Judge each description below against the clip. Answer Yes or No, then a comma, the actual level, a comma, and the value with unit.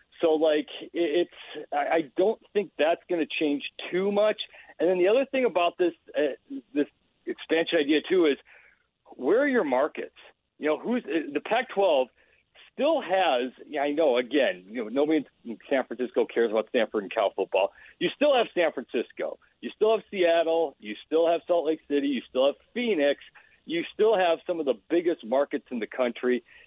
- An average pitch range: No, wide, 7.1 semitones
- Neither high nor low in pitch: Yes, medium, 165 Hz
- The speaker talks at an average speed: Yes, average, 185 wpm